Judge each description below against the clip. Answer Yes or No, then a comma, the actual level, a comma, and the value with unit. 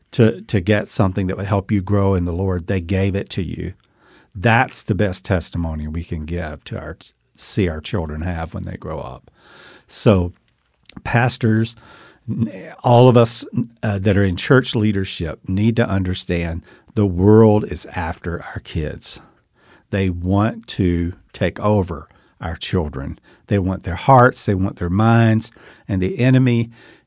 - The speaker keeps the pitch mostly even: No, average, 3.8 semitones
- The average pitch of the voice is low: Yes, low, 100 Hz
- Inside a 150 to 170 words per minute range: Yes, average, 160 wpm